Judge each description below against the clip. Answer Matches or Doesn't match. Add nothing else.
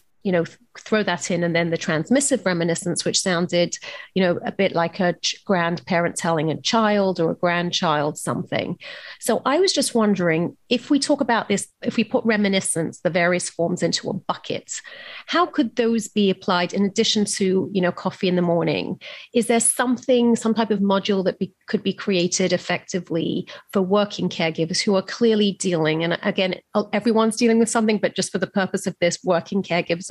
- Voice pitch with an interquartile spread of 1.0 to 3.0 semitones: Doesn't match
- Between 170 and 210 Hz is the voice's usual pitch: Matches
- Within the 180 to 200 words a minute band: Matches